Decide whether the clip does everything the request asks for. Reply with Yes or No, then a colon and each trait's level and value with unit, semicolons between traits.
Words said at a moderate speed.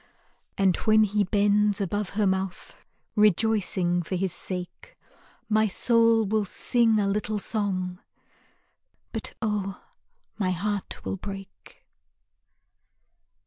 No: slow, 105 wpm